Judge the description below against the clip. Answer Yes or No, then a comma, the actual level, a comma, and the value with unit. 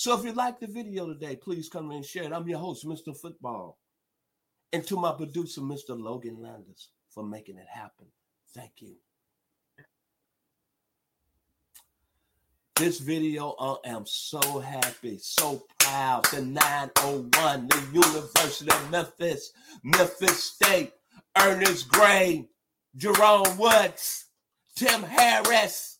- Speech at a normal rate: No, slow, 120 wpm